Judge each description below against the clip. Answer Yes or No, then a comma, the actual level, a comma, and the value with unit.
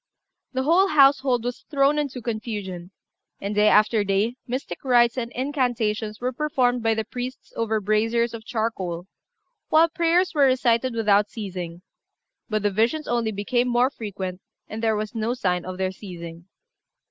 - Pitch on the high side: Yes, high, 230 Hz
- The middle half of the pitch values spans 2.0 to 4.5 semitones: Yes, average, 3.7 semitones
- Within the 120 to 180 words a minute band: Yes, average, 160 wpm